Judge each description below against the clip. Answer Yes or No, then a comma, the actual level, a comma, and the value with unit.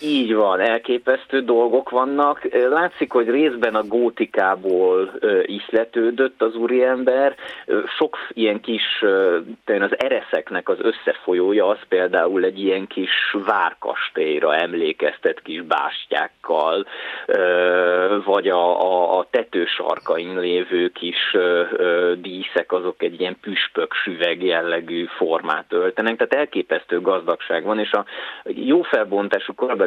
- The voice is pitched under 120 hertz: No, low, 125 Hz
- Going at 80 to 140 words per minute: Yes, average, 110 wpm